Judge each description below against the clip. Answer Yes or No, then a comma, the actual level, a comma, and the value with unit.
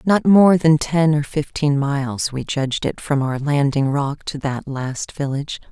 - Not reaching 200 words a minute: Yes, average, 190 wpm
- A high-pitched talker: No, medium, 145 Hz